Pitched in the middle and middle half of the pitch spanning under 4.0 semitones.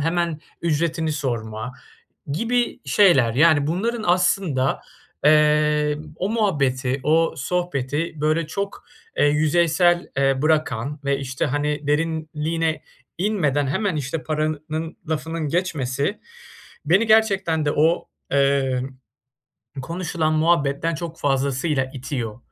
Yes: medium, 155 Hz; average, 3.1 semitones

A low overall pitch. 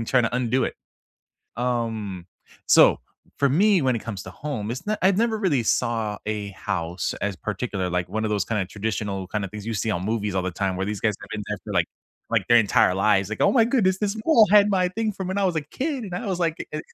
Yes: low, 115 Hz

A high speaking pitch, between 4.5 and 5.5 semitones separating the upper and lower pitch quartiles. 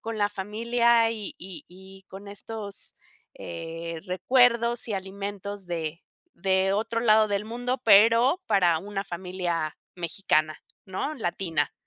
No: high, 200 Hz; average, 3.9 semitones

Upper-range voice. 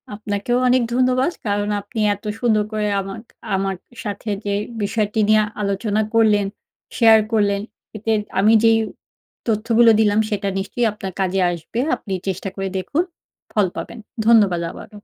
Yes: high, 210 Hz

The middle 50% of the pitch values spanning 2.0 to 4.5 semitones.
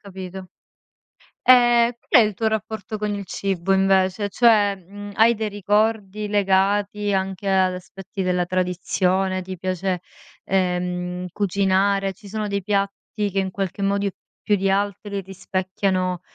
No: narrow, 1.6 semitones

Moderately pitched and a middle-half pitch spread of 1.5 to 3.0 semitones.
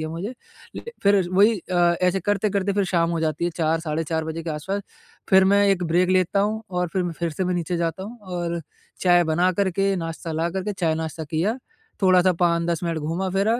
Yes: medium, 180 Hz; average, 2.7 semitones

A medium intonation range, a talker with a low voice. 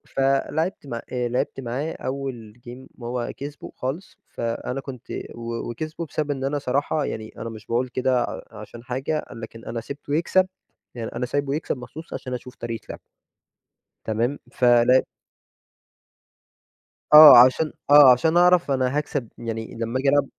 Yes: average, 3.4 semitones; low, 130 Hz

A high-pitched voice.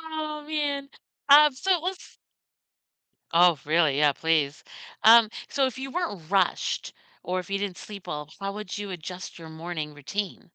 Yes: high, 195 Hz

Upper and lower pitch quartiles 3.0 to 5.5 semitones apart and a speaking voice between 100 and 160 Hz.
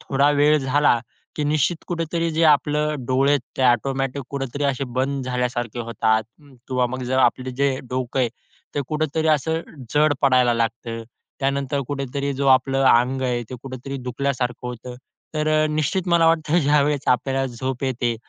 No: narrow, 2.6 semitones; low, 135 Hz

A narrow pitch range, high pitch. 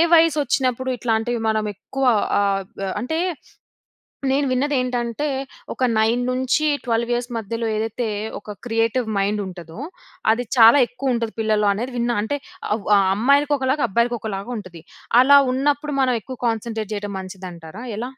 No: average, 3.4 semitones; high, 235 Hz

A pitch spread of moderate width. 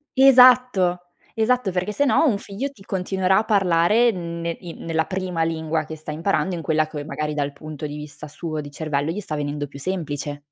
Yes: average, 4.3 semitones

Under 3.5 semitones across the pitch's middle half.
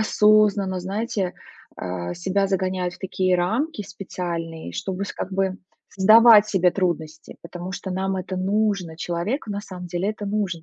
Yes: narrow, 2.5 semitones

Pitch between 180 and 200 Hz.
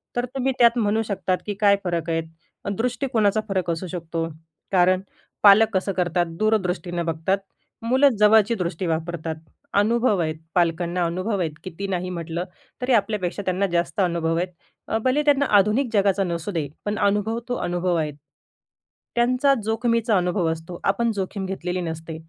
Yes: high, 190 Hz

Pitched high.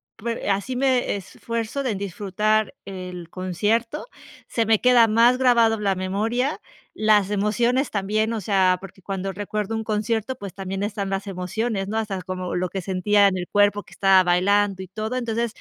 Yes: high, 205 Hz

